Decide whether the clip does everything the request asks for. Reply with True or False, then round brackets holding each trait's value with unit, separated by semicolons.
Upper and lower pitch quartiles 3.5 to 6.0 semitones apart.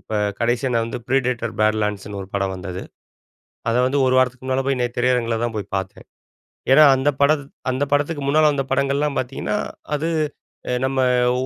True (3.9 semitones)